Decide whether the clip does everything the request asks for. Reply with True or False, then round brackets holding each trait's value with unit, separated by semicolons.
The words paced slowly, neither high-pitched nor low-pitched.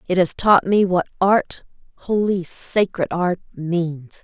True (115 wpm; 180 Hz)